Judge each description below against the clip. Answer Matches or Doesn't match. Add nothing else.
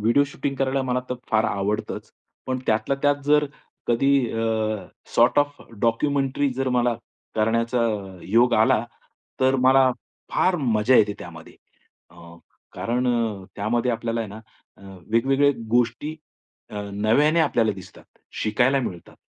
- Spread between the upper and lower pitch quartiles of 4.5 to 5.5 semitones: Doesn't match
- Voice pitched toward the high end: Doesn't match